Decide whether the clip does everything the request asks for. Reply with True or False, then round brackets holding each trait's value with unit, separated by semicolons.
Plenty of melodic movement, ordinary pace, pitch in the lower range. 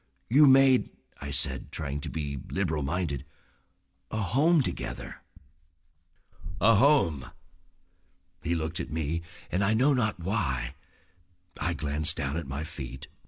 False (7.4 semitones; 130 wpm; 85 Hz)